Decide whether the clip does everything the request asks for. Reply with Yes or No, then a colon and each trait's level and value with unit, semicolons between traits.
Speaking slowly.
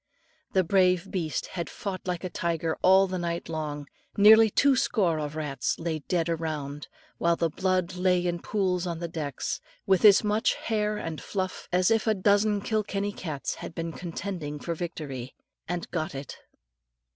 No: average, 170 wpm